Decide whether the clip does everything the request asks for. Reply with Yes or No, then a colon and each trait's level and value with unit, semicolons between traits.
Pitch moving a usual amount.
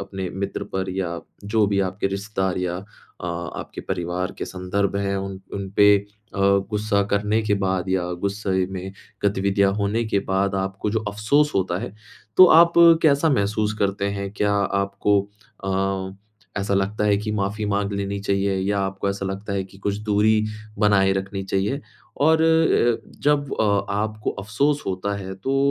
No: narrow, 1.6 semitones